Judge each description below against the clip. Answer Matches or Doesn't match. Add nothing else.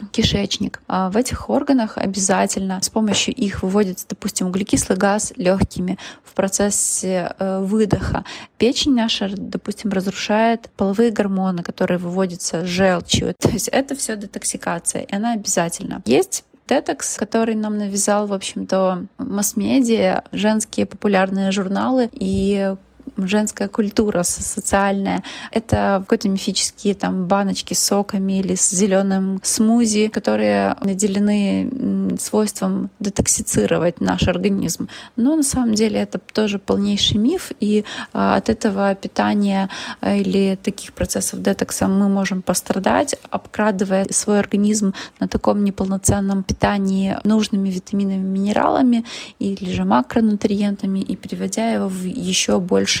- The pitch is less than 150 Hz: Doesn't match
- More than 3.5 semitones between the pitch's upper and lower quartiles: Doesn't match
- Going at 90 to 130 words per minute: Matches